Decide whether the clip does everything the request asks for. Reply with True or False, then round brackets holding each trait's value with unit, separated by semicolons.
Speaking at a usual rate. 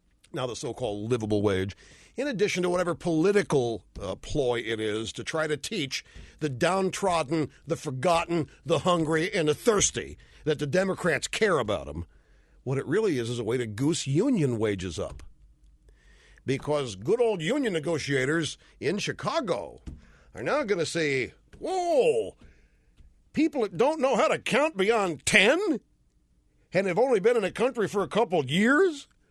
True (165 wpm)